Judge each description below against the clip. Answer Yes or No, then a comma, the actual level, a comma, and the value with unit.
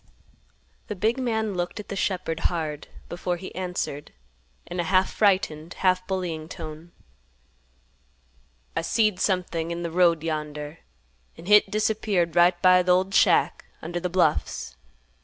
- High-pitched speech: No, medium, 180 Hz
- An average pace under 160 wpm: Yes, average, 140 wpm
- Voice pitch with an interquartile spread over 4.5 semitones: No, narrow, 2.4 semitones